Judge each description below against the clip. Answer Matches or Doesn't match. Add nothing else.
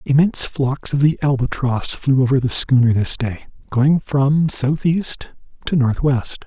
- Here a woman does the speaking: Doesn't match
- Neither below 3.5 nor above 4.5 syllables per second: Matches